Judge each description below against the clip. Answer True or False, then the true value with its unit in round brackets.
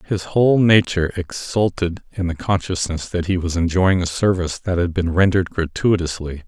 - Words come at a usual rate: True (165 wpm)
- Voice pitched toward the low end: True (90 Hz)